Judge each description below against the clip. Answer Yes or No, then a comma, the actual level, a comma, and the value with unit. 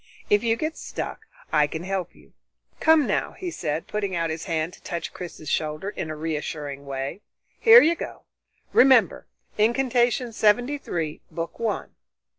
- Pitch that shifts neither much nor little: No, wide, 7.4 semitones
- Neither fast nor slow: Yes, average, 160 wpm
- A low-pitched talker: No, high, 190 Hz